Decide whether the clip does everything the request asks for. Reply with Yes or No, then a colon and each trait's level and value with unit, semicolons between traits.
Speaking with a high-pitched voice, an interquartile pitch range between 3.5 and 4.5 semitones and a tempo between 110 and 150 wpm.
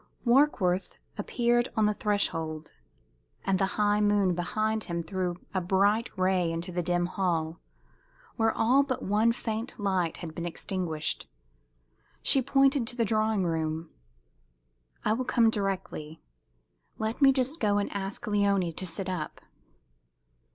Yes: high, 200 Hz; average, 4.1 semitones; average, 140 wpm